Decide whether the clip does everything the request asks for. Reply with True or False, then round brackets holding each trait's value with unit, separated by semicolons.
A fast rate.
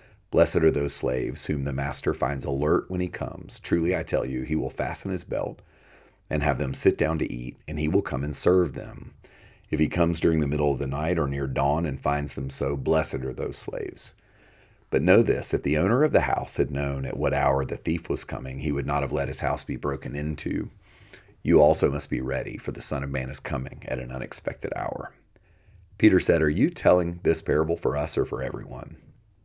True (225 wpm)